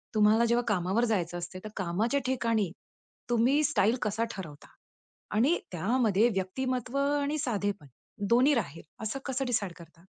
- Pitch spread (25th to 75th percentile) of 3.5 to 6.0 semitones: Yes, average, 5.1 semitones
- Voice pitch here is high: Yes, high, 220 Hz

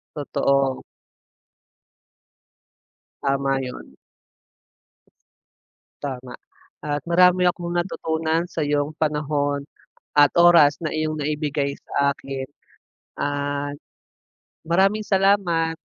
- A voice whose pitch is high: No, medium, 150 Hz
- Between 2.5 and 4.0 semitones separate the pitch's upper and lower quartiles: Yes, average, 3.0 semitones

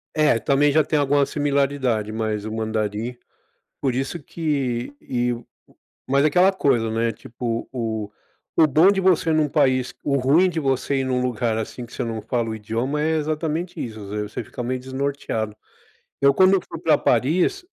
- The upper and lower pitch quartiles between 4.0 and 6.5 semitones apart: Yes, average, 4.7 semitones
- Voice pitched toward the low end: Yes, low, 130 Hz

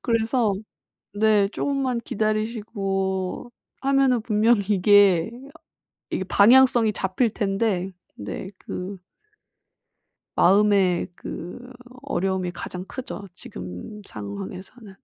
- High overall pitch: Yes, high, 205 Hz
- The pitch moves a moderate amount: Yes, average, 3.5 semitones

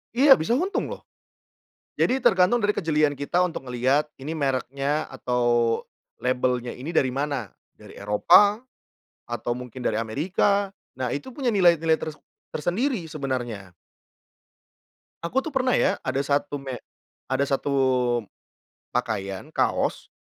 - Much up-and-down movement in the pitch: Yes, wide, 6.5 semitones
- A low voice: No, medium, 145 Hz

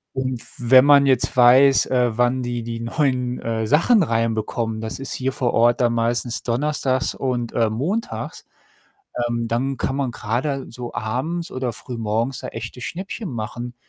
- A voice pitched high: No, low, 125 Hz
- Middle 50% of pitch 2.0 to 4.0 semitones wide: Yes, narrow, 2.4 semitones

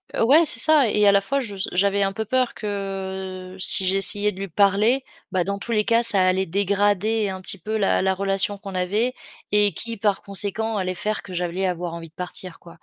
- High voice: Yes, high, 200 Hz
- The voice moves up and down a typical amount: No, narrow, 2.3 semitones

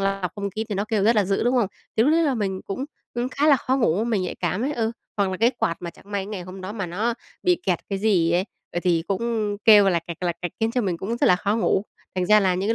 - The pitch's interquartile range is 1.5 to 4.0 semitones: Yes, average, 3.7 semitones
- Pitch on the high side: Yes, high, 205 Hz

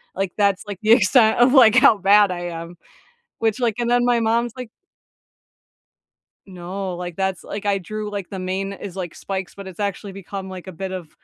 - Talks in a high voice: Yes, high, 195 Hz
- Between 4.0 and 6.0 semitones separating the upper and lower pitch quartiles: No, average, 2.9 semitones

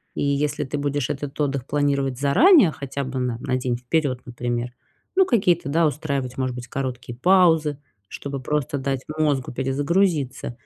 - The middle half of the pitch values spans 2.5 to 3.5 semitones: Yes, average, 2.8 semitones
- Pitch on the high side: No, medium, 140 Hz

